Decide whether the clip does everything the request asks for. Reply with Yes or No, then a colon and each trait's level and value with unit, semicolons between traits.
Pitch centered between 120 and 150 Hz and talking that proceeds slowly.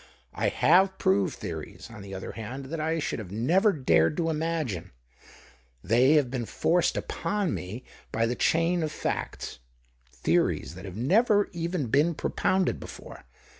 No: low, 135 Hz; average, 165 wpm